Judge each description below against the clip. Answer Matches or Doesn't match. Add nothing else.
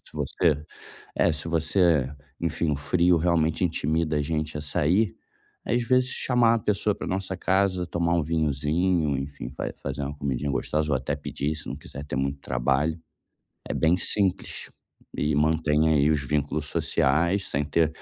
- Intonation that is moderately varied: Matches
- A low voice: Matches